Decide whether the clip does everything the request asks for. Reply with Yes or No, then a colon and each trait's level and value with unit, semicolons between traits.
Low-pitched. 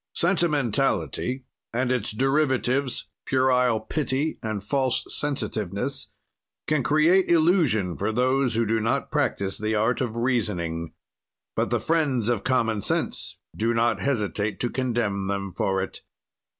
Yes: low, 120 Hz